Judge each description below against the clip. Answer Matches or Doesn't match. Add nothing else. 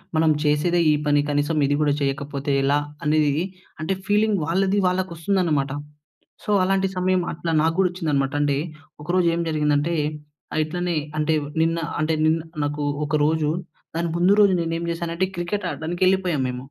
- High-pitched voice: Doesn't match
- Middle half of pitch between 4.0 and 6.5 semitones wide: Doesn't match